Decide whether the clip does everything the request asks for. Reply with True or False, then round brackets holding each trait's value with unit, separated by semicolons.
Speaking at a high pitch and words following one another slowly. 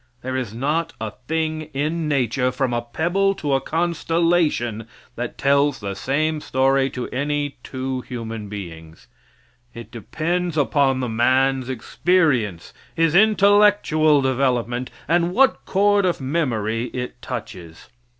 False (135 Hz; 130 wpm)